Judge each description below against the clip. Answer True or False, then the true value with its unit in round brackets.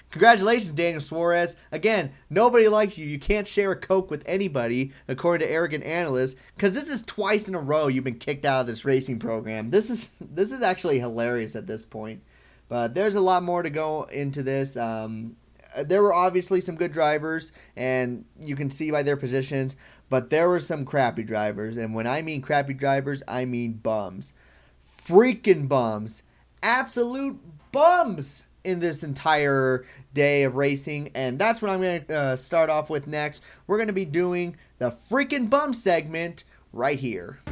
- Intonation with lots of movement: True (6.0 semitones)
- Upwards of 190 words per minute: False (175 wpm)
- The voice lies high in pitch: False (150 Hz)